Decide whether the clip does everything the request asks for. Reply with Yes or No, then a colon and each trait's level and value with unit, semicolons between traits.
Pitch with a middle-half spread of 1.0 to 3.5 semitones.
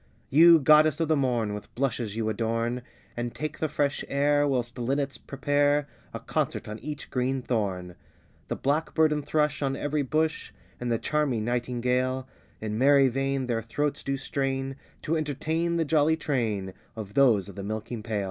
No: average, 3.9 semitones